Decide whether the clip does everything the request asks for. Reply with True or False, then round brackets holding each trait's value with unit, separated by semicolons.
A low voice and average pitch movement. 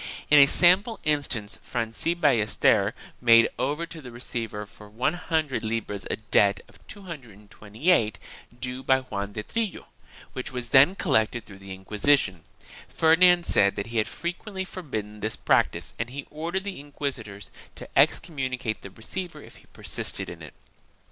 False (125 Hz; 7.0 semitones)